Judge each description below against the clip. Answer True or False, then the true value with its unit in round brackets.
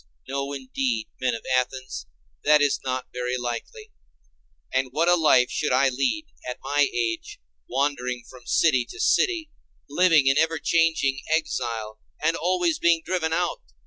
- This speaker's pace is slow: False (150 wpm)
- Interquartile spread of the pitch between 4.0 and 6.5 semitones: True (4.5 semitones)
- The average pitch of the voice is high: False (140 Hz)